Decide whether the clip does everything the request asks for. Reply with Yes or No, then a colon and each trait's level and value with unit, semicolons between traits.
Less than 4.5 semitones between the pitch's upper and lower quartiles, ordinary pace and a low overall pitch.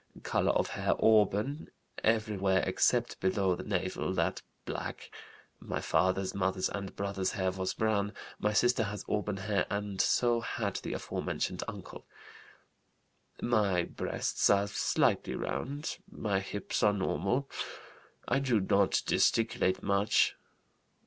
No: narrow, 2.4 semitones; slow, 120 wpm; low, 100 Hz